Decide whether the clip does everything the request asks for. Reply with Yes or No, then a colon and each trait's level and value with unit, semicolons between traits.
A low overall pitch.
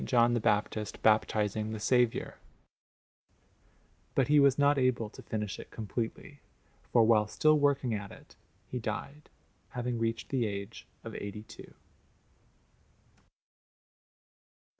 Yes: low, 115 Hz